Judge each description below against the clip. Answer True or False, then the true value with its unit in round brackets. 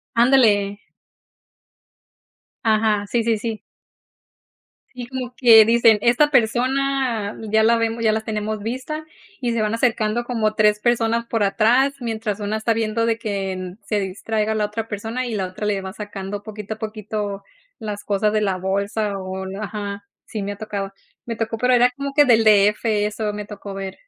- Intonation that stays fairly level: True (2.1 semitones)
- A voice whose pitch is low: False (215 Hz)